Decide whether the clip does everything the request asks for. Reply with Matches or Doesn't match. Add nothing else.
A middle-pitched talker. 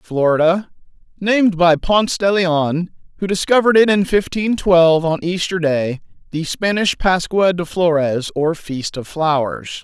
Matches